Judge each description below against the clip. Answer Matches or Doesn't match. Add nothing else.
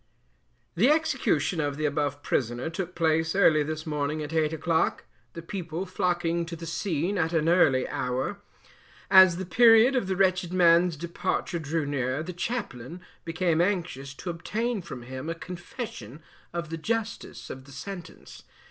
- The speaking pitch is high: Doesn't match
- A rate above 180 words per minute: Doesn't match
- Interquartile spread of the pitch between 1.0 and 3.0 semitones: Doesn't match